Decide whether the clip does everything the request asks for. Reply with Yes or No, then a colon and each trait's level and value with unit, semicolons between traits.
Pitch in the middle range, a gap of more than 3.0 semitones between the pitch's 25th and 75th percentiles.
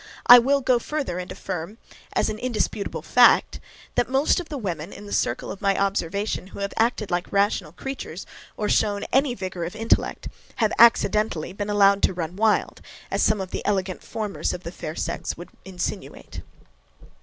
No: high, 200 Hz; average, 3.5 semitones